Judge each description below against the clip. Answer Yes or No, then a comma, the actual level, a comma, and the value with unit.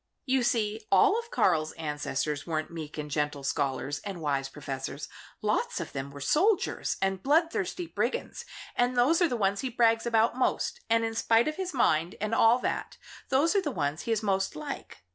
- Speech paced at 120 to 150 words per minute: No, average, 190 wpm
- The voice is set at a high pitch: Yes, high, 215 Hz